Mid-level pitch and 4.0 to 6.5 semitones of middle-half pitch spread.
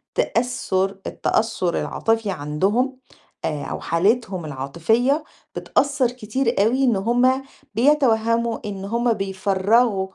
No: high, 225 Hz; average, 4.4 semitones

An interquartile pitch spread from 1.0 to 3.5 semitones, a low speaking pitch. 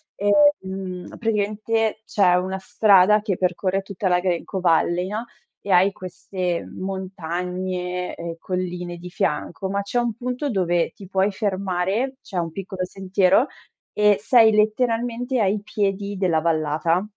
No: average, 2.8 semitones; high, 190 Hz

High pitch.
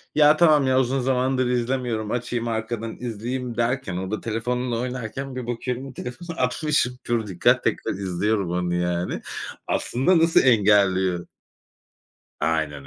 No: low, 120 Hz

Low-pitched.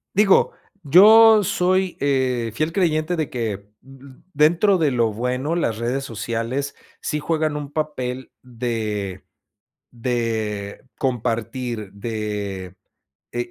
Yes: low, 125 Hz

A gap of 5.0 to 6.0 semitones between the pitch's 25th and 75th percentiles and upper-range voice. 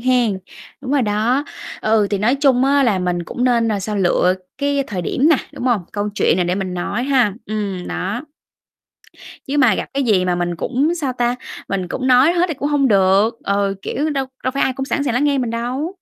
Yes: wide, 5.4 semitones; high, 240 Hz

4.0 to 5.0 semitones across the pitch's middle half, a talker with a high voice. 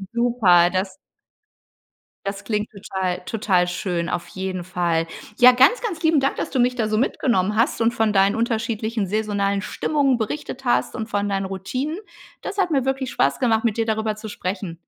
Yes: average, 4.4 semitones; high, 215 Hz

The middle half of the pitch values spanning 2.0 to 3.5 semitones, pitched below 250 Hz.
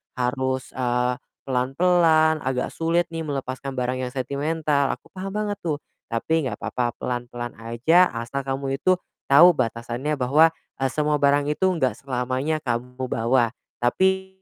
No: average, 4.1 semitones; low, 135 Hz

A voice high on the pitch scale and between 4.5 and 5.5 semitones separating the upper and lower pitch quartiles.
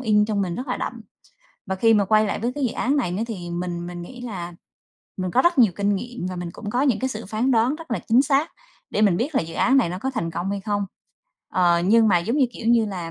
Yes: high, 215 Hz; average, 5.2 semitones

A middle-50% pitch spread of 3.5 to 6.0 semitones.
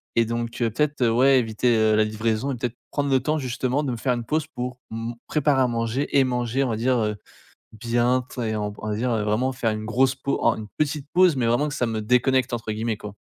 No: average, 2.9 semitones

